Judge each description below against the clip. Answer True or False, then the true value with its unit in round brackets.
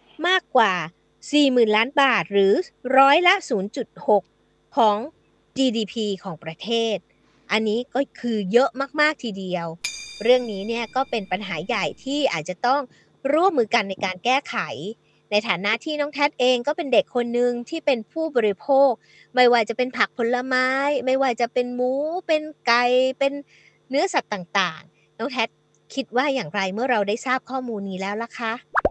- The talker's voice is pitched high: True (245 Hz)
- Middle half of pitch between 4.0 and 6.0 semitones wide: True (4.7 semitones)